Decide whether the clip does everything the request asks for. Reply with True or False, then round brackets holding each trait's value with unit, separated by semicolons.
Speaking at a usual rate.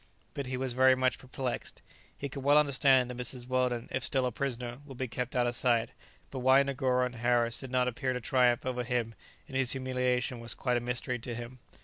False (225 wpm)